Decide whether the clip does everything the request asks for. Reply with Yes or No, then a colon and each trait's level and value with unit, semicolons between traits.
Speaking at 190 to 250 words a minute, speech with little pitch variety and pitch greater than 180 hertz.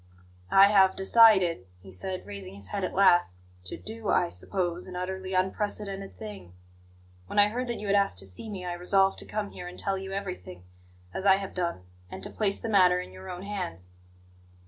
Yes: fast, 205 wpm; narrow, 2.2 semitones; high, 190 Hz